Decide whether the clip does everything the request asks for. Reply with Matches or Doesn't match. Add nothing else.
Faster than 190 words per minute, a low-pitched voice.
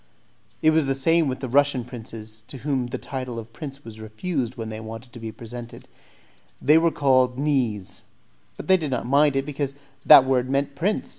Matches